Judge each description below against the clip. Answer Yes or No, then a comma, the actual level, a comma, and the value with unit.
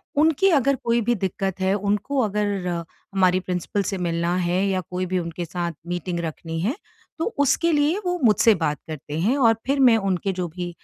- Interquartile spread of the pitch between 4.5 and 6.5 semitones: Yes, average, 5.0 semitones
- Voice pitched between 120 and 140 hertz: No, high, 190 Hz